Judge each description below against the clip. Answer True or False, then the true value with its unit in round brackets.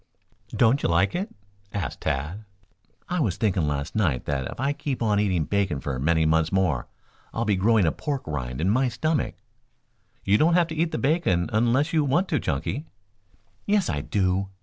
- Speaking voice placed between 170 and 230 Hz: False (100 Hz)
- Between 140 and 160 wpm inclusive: False (190 wpm)